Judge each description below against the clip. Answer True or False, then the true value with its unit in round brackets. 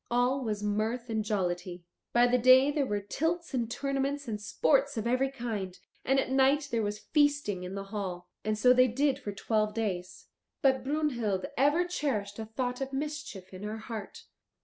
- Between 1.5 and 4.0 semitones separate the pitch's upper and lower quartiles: False (4.7 semitones)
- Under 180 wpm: False (185 wpm)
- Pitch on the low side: False (240 Hz)